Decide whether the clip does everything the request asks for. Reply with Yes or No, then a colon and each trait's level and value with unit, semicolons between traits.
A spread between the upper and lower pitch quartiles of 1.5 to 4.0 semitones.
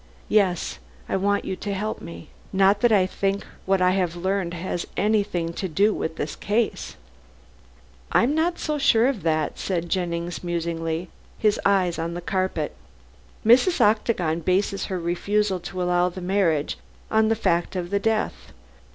Yes: average, 3.3 semitones